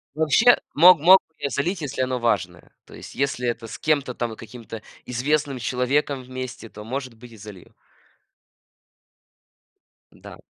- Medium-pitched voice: No, low, 130 Hz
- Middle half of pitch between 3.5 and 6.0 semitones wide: Yes, average, 3.9 semitones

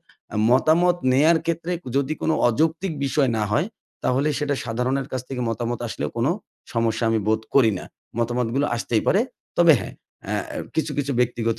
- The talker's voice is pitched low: Yes, low, 130 Hz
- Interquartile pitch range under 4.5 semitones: No, average, 5.0 semitones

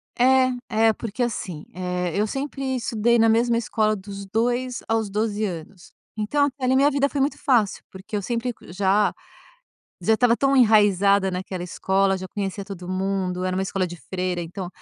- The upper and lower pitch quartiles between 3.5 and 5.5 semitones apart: Yes, average, 4.2 semitones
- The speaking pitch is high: Yes, high, 210 Hz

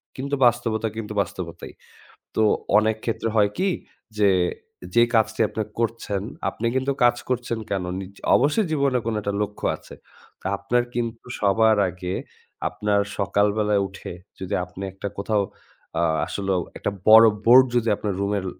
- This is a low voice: Yes, low, 110 Hz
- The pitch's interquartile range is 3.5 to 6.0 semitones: No, average, 2.9 semitones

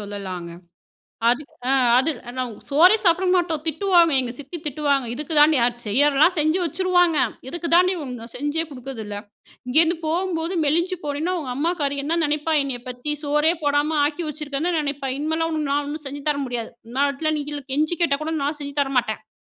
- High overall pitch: Yes, very high, 295 Hz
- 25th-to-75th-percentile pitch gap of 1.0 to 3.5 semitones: Yes, average, 2.9 semitones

